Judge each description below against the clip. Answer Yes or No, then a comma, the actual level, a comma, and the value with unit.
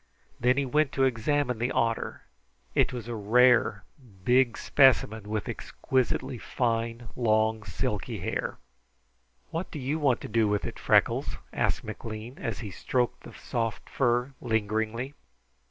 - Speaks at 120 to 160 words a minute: Yes, average, 140 wpm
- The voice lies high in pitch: No, low, 120 Hz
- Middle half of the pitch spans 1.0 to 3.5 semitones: Yes, average, 2.8 semitones